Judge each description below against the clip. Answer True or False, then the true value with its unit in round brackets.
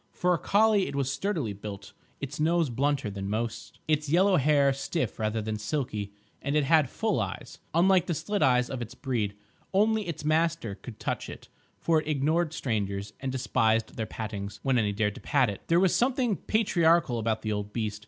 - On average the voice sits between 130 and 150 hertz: True (135 Hz)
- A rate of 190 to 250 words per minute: True (195 wpm)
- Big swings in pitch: True (7.3 semitones)